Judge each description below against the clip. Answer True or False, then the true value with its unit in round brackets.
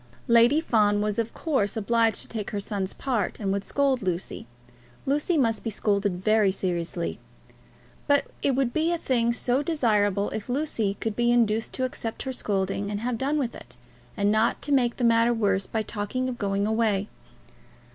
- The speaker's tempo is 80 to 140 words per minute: False (180 wpm)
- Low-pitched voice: False (225 Hz)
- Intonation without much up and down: False (3.8 semitones)